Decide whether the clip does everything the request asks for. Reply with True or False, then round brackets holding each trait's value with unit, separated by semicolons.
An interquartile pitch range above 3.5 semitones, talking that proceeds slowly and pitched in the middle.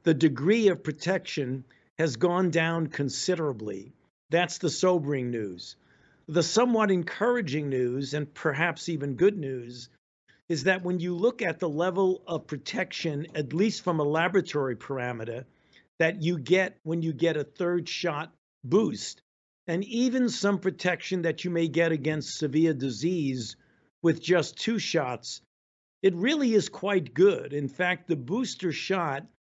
False (4.0 semitones; 145 wpm; 165 Hz)